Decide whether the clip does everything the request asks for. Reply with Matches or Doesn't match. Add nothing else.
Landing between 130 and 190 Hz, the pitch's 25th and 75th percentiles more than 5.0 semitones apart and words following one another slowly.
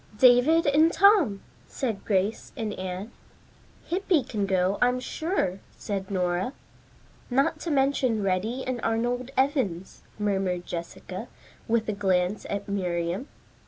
Doesn't match